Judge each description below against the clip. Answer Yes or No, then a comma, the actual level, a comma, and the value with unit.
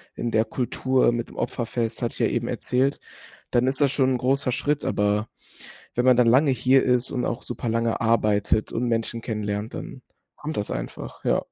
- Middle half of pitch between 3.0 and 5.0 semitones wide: No, narrow, 2.5 semitones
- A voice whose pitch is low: Yes, low, 120 Hz